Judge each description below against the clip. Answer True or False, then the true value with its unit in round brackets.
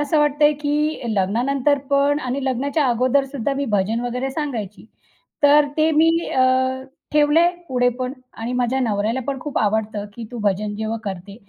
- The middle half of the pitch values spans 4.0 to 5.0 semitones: True (4.6 semitones)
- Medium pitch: False (260 Hz)